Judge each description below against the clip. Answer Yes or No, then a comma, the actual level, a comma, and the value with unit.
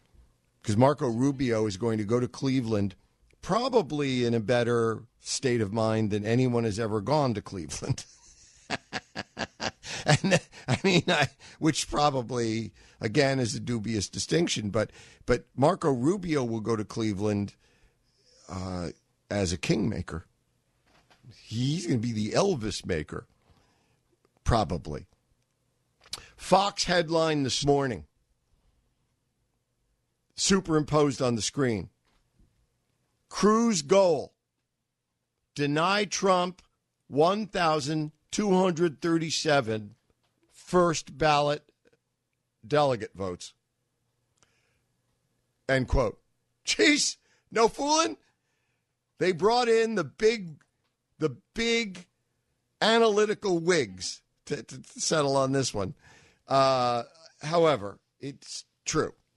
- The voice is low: Yes, low, 130 Hz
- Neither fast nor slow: No, slow, 95 wpm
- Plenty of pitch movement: Yes, wide, 6.2 semitones